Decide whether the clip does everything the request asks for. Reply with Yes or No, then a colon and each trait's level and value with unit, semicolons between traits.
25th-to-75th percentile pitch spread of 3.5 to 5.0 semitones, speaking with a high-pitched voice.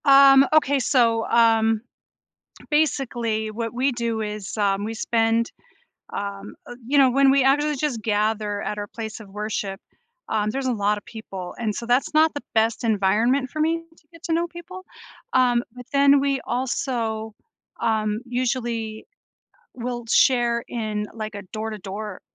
Yes: average, 3.8 semitones; high, 230 Hz